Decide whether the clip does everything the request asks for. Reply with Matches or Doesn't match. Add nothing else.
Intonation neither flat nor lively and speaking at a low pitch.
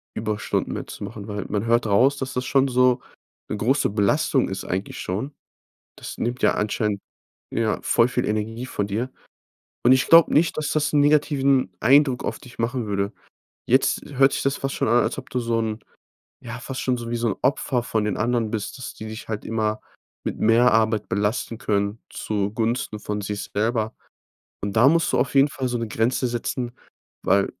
Matches